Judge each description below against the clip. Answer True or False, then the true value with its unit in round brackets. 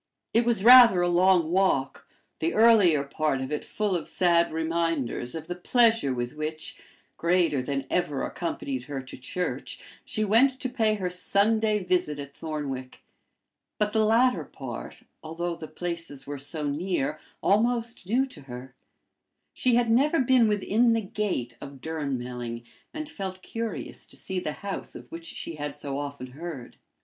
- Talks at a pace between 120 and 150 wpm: False (160 wpm)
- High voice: False (175 Hz)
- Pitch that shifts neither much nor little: False (7.0 semitones)